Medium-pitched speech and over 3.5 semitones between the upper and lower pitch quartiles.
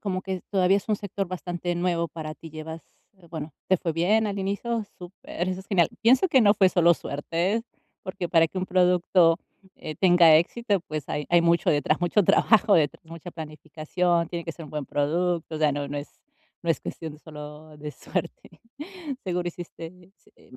No: medium, 175 Hz; average, 2.8 semitones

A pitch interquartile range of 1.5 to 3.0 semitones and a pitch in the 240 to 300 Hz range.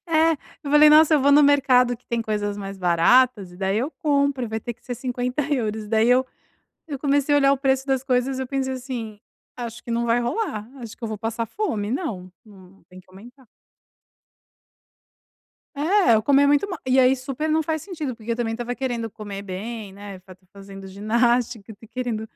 No: average, 4.3 semitones; high, 245 Hz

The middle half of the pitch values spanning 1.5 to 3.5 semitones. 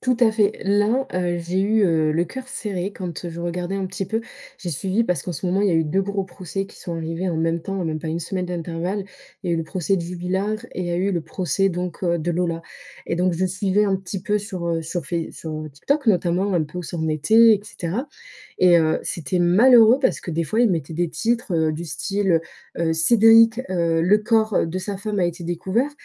Yes: average, 3.2 semitones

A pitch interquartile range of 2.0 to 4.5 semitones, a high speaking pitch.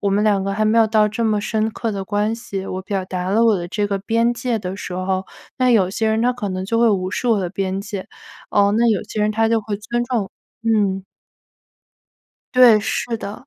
Yes: narrow, 2.6 semitones; high, 210 Hz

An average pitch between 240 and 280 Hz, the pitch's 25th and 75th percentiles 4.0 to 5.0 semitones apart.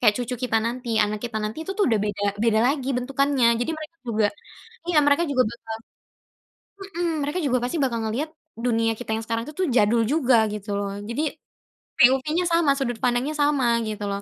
Yes: high, 245 Hz; average, 4.3 semitones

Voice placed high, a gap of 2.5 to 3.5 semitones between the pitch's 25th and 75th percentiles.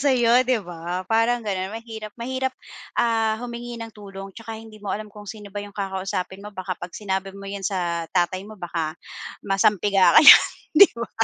Yes: high, 205 Hz; average, 3.1 semitones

